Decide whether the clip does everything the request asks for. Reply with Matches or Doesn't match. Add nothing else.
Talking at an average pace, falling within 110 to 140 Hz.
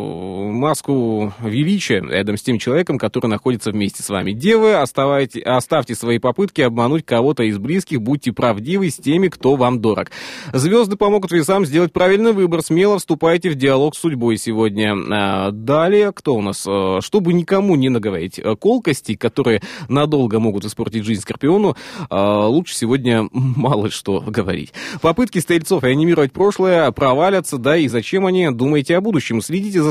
Matches